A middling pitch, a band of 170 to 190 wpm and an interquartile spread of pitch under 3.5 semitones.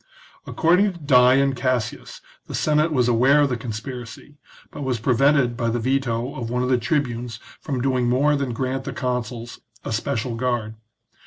No: low, 125 Hz; average, 175 wpm; narrow, 2.6 semitones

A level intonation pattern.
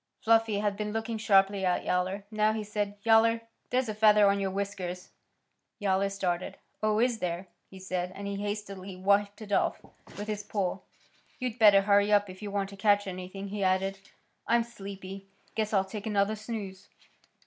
Yes: narrow, 1.8 semitones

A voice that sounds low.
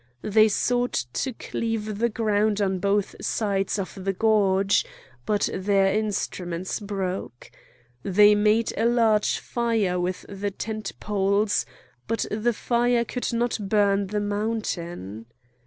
No: high, 205 Hz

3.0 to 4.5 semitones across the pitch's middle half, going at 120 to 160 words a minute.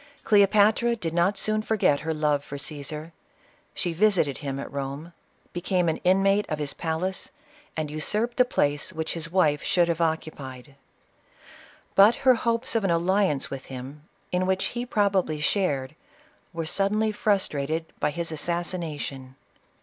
No: average, 4.9 semitones; average, 150 wpm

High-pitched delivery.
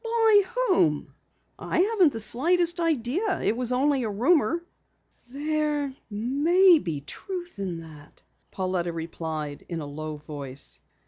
Yes: very high, 250 Hz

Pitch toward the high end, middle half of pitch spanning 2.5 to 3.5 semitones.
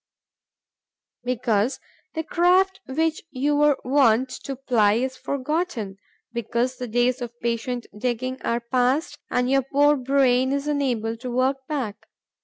Yes: very high, 255 Hz; average, 2.8 semitones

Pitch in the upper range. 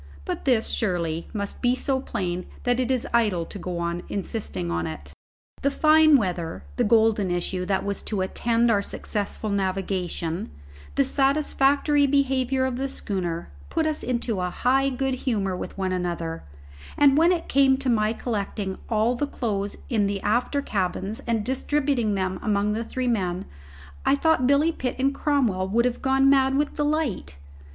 Yes: high, 225 Hz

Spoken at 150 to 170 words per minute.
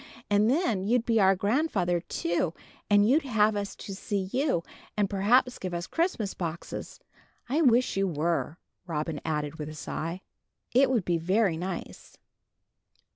Yes: average, 155 wpm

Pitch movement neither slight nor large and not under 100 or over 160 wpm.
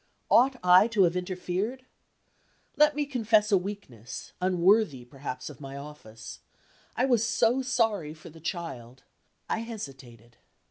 No: wide, 8.4 semitones; slow, 135 wpm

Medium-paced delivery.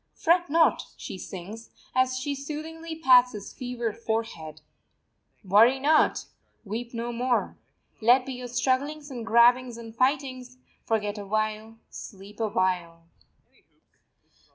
No: slow, 125 wpm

